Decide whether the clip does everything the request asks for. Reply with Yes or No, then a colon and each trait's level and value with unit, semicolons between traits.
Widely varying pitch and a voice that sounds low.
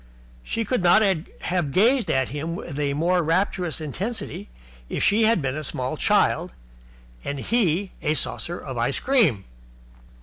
No: wide, 6.3 semitones; medium, 170 Hz